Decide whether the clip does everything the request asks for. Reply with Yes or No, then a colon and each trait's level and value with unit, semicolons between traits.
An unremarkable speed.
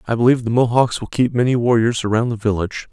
No: fast, 225 wpm